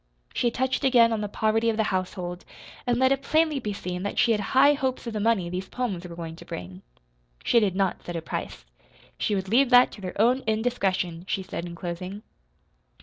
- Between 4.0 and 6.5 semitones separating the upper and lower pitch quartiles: Yes, average, 5.2 semitones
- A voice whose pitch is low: No, high, 210 Hz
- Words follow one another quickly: Yes, fast, 215 wpm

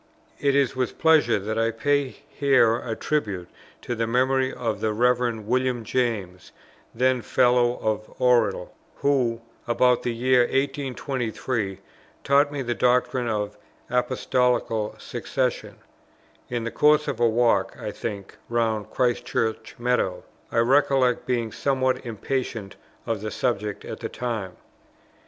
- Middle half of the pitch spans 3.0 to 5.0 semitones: No, narrow, 2.6 semitones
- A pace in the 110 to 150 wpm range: Yes, slow, 135 wpm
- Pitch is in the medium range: No, low, 120 Hz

